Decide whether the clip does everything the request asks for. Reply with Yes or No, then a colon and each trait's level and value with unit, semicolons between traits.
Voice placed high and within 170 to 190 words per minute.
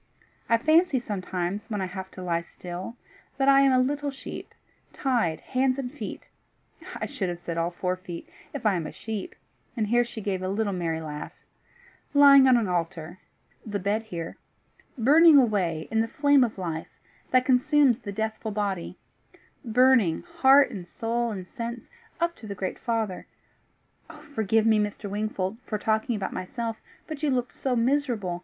Yes: high, 220 Hz; average, 175 wpm